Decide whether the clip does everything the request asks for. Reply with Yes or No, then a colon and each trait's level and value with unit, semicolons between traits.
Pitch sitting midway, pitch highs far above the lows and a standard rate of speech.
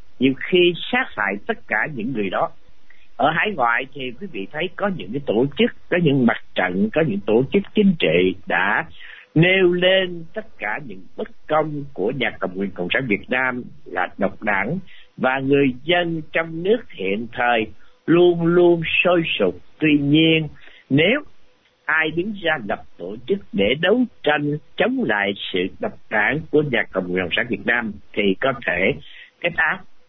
Yes: medium, 155 Hz; wide, 6.7 semitones; average, 180 wpm